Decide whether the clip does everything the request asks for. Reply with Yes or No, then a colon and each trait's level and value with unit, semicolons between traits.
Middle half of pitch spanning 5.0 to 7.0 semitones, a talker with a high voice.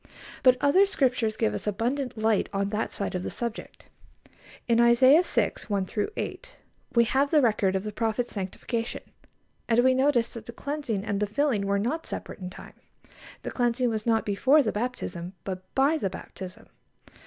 No: average, 3.9 semitones; high, 230 Hz